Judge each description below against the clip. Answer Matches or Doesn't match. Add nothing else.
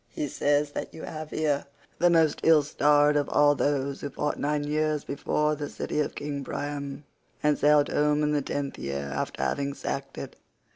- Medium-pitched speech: Matches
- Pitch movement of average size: Doesn't match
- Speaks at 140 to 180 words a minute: Doesn't match